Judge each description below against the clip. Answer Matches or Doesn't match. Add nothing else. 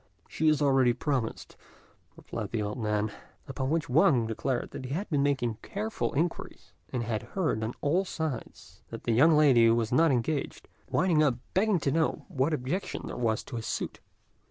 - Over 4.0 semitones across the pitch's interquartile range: Matches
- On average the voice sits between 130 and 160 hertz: Matches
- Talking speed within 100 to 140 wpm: Doesn't match